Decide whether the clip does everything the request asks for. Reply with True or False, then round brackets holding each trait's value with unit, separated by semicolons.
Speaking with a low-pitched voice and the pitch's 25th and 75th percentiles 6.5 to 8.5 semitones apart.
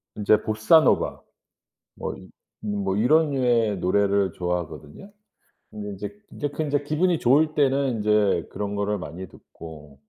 True (105 Hz; 6.9 semitones)